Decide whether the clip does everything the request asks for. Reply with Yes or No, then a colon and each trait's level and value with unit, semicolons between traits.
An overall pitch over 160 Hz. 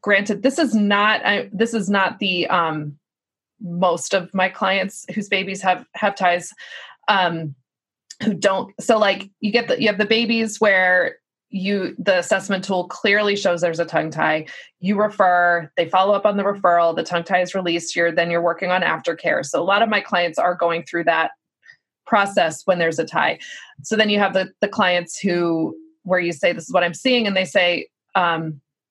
Yes: high, 190 Hz